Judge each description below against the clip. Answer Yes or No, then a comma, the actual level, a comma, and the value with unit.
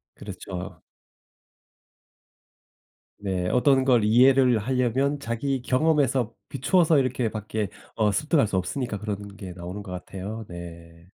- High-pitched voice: No, low, 115 Hz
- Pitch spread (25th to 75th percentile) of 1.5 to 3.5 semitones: No, average, 5.2 semitones